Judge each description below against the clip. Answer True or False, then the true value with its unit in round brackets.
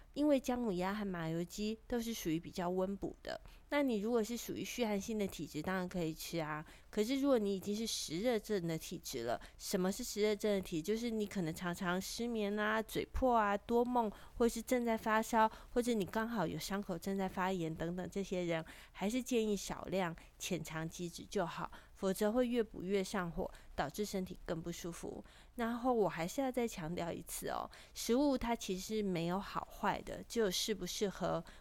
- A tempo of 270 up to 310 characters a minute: True (295 characters per minute)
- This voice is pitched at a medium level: False (200 Hz)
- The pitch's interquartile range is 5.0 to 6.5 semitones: False (4.3 semitones)